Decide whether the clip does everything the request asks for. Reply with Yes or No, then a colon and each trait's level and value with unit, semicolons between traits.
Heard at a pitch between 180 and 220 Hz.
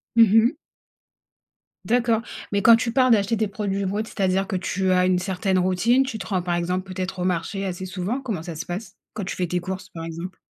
Yes: high, 190 Hz